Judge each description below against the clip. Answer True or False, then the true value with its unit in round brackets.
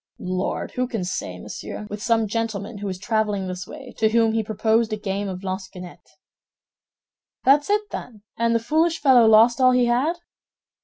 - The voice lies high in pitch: True (220 Hz)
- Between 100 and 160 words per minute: False (175 wpm)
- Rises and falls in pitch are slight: False (3.5 semitones)